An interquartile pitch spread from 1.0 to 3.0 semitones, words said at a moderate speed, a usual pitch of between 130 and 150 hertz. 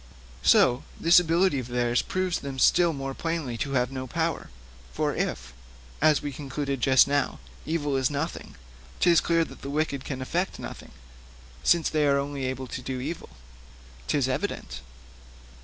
No: average, 3.7 semitones; average, 160 wpm; medium, 140 Hz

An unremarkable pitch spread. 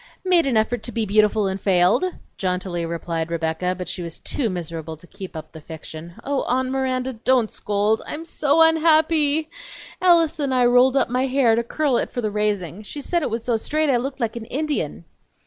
No: wide, 7.1 semitones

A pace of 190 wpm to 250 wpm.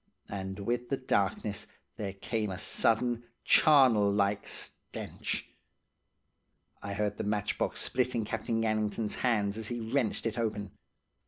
No: slow, 135 wpm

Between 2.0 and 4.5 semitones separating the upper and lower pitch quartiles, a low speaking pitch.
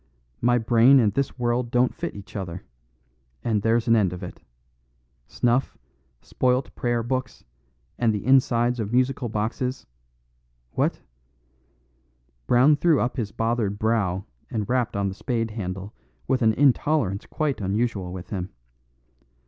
Yes: average, 3.9 semitones; low, 115 Hz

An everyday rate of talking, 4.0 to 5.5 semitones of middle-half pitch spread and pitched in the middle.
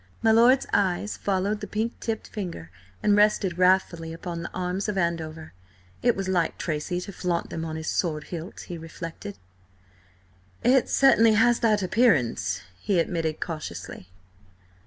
Yes: average, 150 wpm; average, 4.3 semitones; medium, 180 Hz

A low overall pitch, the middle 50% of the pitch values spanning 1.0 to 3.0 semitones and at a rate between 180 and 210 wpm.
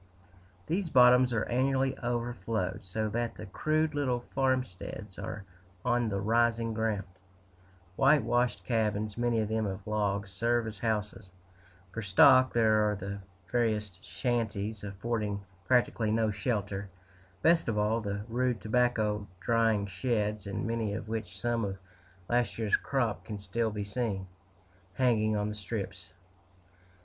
No: low, 110 Hz; average, 2.7 semitones; average, 140 wpm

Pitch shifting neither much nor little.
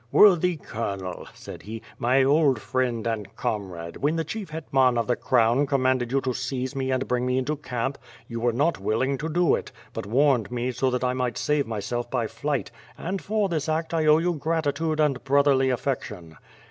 Yes: average, 3.9 semitones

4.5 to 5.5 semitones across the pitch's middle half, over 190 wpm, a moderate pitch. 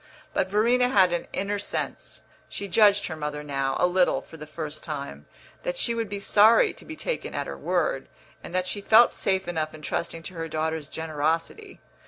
Yes: average, 4.8 semitones; average, 200 wpm; medium, 180 Hz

